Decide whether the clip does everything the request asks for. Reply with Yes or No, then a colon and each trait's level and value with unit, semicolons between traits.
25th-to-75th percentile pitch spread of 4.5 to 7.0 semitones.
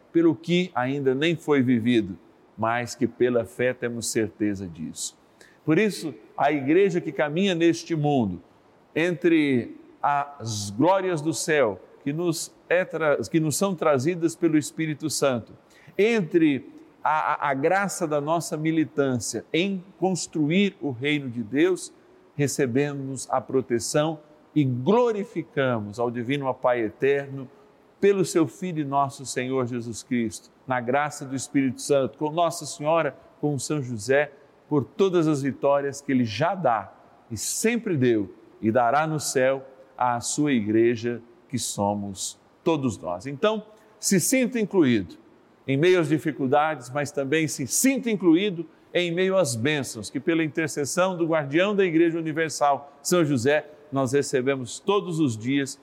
Yes: average, 4.8 semitones